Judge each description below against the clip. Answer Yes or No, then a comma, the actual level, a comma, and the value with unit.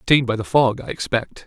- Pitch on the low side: Yes, low, 120 Hz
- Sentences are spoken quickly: Yes, fast, 245 wpm